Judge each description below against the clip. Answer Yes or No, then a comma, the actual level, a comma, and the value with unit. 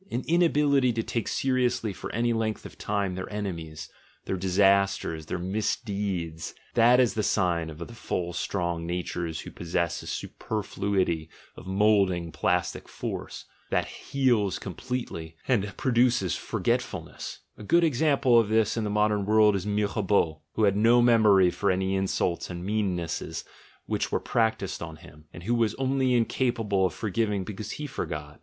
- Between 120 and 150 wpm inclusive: No, average, 160 wpm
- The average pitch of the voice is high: No, low, 100 Hz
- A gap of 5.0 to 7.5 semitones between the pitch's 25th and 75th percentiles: No, average, 4.5 semitones